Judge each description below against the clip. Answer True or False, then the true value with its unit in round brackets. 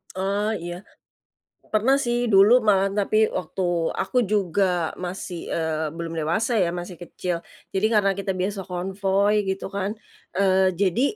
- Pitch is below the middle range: False (195 Hz)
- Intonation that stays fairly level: True (2.3 semitones)